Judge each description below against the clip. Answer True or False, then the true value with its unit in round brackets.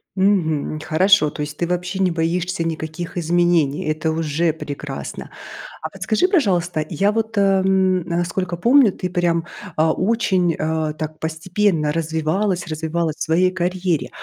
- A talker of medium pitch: True (170 Hz)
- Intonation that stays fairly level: False (3.0 semitones)